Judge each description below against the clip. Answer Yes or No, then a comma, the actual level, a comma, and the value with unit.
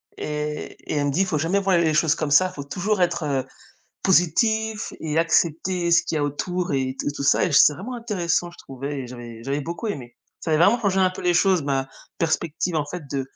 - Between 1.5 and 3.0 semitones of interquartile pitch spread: No, average, 4.3 semitones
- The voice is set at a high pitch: No, medium, 165 Hz